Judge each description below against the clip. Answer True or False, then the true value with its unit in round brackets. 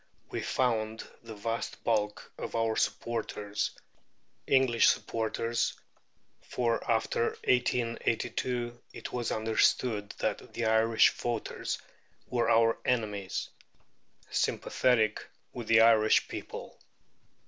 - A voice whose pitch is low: True (115 Hz)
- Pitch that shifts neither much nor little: False (1.5 semitones)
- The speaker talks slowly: True (95 wpm)